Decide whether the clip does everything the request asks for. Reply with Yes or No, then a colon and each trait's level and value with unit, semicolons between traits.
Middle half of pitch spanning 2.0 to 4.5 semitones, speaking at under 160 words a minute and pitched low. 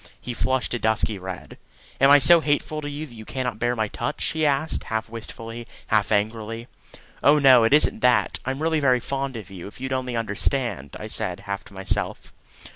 No: average, 3.9 semitones; average, 200 wpm; low, 120 Hz